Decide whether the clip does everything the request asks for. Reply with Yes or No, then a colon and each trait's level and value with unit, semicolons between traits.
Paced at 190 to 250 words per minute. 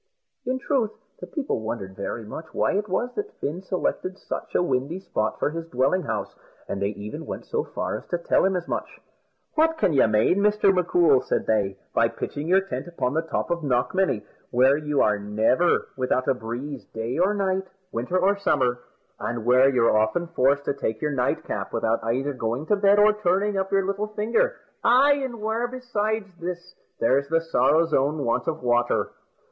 Yes: average, 195 wpm